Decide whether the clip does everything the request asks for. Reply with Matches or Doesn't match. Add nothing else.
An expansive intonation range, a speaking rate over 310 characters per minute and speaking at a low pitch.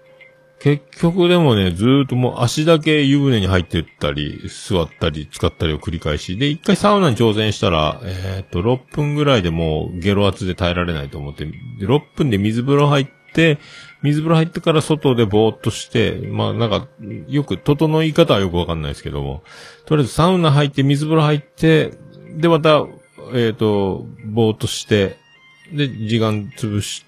Matches